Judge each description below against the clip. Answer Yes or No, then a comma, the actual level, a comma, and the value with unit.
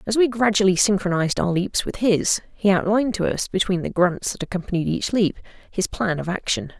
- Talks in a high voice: Yes, high, 195 Hz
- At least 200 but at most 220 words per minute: Yes, fast, 205 wpm